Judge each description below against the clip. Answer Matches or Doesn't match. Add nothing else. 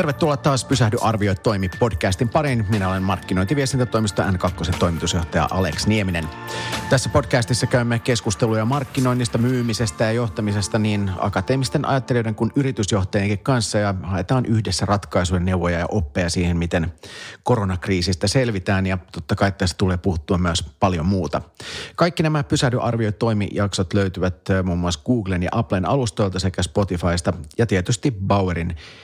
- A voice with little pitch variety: Doesn't match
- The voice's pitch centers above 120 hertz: Doesn't match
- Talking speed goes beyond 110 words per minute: Matches